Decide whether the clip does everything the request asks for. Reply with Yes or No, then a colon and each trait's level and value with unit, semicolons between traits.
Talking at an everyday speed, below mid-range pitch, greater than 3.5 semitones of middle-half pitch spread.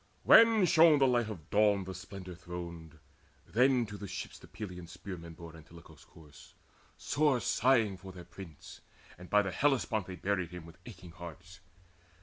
Yes: average, 165 wpm; very low, 95 Hz; average, 4.3 semitones